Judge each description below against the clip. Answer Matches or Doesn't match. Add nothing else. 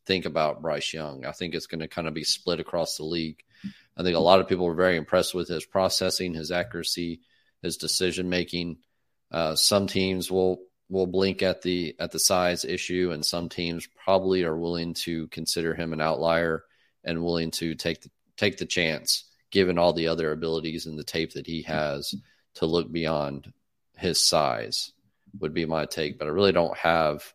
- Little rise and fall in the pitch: Matches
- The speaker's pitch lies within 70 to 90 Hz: Matches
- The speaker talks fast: Doesn't match